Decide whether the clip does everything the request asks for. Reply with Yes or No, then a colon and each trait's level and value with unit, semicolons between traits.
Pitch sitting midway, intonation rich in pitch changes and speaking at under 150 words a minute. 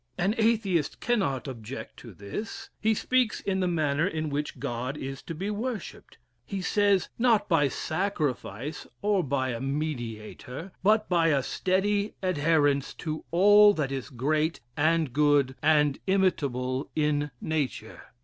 Yes: medium, 155 Hz; wide, 6.0 semitones; average, 140 wpm